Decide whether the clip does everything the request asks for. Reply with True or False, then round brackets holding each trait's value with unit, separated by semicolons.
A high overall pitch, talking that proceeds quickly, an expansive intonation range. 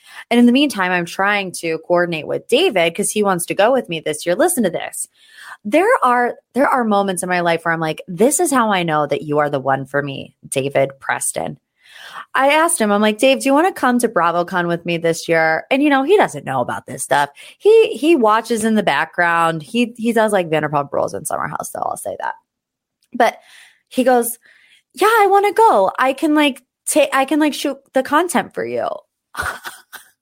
True (225 Hz; 220 wpm; 9.0 semitones)